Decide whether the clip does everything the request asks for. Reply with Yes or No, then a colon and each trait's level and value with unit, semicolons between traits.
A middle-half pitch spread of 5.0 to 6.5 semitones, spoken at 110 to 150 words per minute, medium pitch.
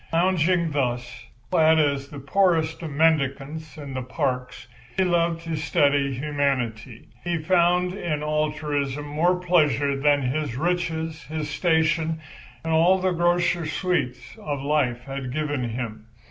No: average, 3.3 semitones; slow, 135 wpm; medium, 150 Hz